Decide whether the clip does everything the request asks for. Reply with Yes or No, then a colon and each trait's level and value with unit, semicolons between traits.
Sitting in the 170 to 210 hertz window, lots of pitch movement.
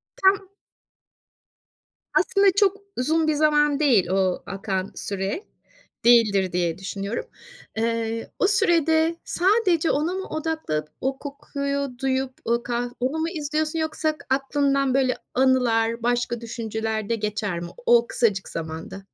No: very high, 255 Hz; wide, 5.9 semitones